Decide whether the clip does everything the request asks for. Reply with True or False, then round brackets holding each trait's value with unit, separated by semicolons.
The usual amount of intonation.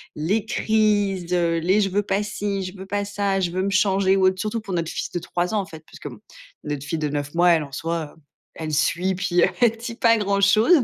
True (3.4 semitones)